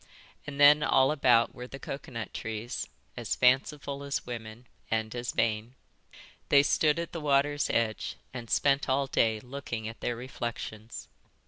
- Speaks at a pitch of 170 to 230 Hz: No, low, 125 Hz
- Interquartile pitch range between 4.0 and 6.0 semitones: No, average, 3.4 semitones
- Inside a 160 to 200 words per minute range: No, average, 150 wpm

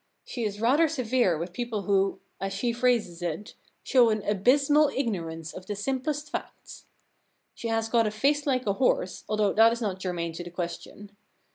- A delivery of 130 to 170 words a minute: No, average, 180 wpm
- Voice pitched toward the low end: No, high, 215 Hz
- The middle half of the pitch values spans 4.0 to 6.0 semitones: Yes, average, 4.9 semitones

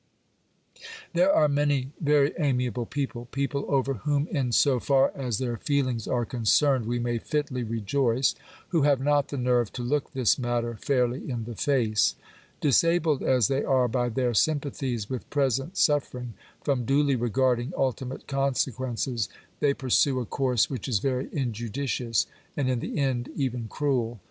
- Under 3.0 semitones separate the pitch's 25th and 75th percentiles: Yes, narrow, 2.6 semitones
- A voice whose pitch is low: Yes, low, 130 Hz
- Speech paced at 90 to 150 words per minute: No, average, 160 wpm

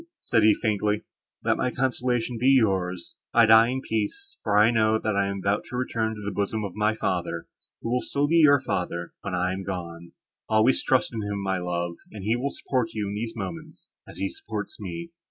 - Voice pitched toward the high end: No, low, 110 Hz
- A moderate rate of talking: No, fast, 215 wpm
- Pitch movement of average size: Yes, average, 4.0 semitones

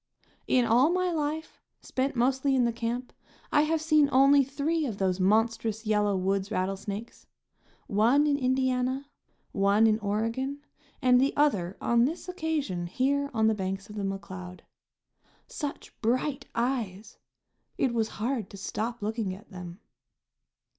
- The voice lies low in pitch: No, high, 235 Hz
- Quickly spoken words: No, average, 145 wpm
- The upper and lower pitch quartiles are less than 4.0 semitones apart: No, average, 5.3 semitones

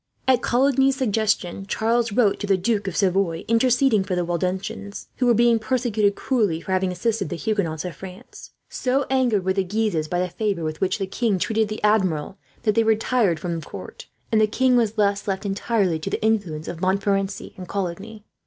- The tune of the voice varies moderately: Yes, average, 3.4 semitones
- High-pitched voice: Yes, high, 205 Hz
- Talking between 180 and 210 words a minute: Yes, average, 195 wpm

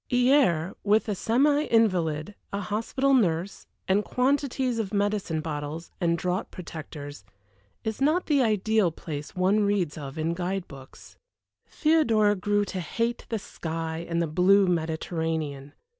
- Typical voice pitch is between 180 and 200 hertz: Yes, high, 190 Hz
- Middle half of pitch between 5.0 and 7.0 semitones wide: Yes, wide, 5.4 semitones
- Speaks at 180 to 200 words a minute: No, average, 140 wpm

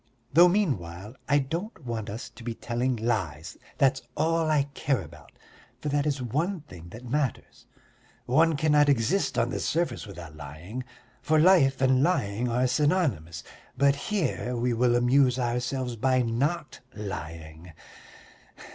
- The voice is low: Yes, low, 125 Hz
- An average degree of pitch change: Yes, average, 4.9 semitones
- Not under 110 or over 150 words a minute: Yes, average, 145 wpm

